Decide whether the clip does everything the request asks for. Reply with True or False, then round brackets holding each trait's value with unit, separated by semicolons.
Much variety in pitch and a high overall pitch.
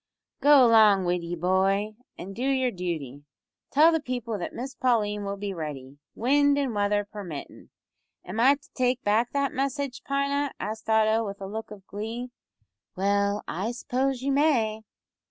False (4.8 semitones; 220 Hz)